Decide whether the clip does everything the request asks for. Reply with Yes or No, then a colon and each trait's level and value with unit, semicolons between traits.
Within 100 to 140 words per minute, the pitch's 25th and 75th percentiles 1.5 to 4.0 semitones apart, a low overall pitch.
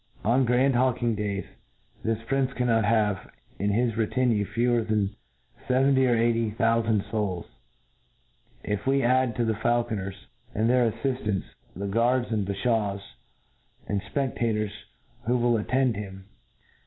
Yes: slow, 135 wpm; average, 3.0 semitones; low, 115 Hz